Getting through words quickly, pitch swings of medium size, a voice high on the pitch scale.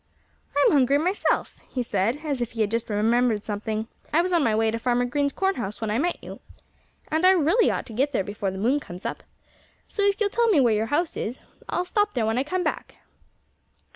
No: fast, 230 wpm; wide, 7.2 semitones; very high, 250 Hz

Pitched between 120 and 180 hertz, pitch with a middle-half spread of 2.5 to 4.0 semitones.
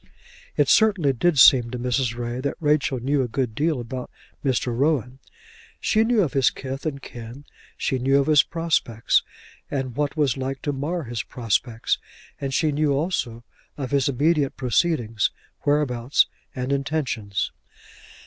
Yes: low, 135 Hz; average, 3.3 semitones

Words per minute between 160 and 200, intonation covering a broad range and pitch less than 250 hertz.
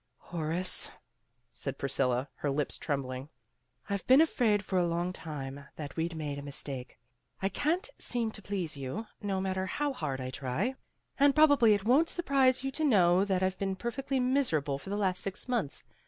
Yes: average, 185 wpm; wide, 9.0 semitones; high, 190 Hz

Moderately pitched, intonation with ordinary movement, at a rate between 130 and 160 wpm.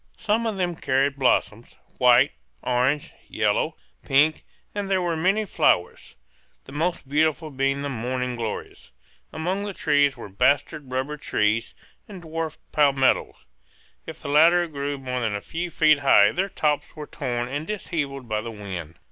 Yes: medium, 145 Hz; average, 4.4 semitones; average, 155 wpm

